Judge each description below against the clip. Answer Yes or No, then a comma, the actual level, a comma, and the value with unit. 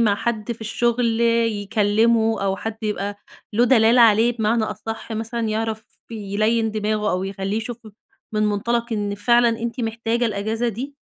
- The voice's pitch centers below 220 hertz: No, high, 225 Hz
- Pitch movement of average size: No, narrow, 1.8 semitones